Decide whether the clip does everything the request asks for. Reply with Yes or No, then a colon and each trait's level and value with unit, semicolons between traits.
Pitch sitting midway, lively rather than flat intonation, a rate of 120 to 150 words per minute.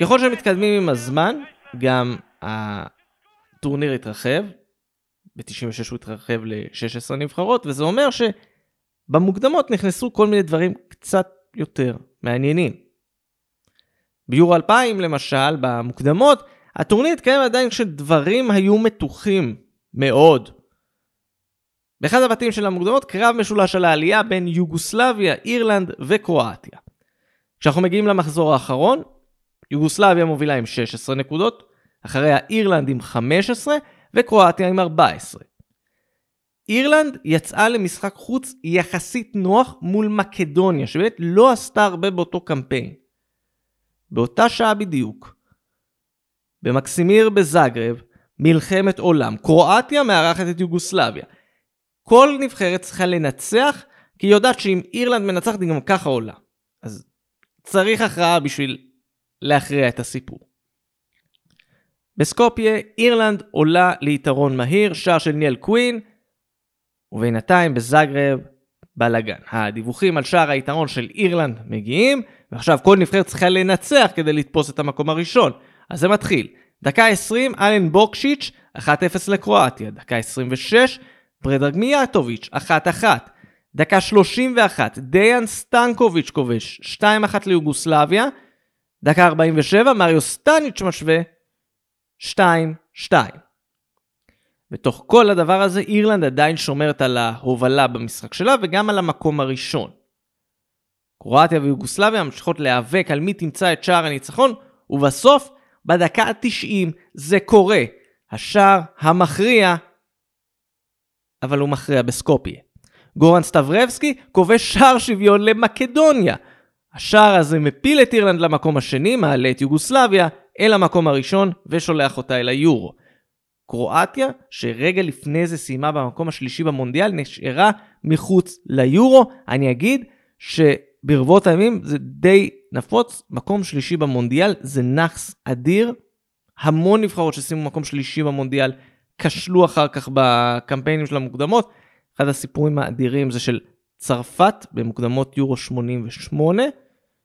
No: medium, 170 Hz; wide, 7.1 semitones; average, 110 wpm